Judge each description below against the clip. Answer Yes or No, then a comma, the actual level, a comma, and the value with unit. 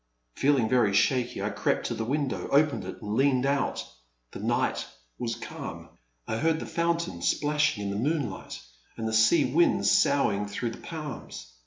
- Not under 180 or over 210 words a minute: No, average, 170 wpm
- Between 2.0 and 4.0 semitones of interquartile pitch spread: No, average, 5.2 semitones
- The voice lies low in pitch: Yes, low, 130 Hz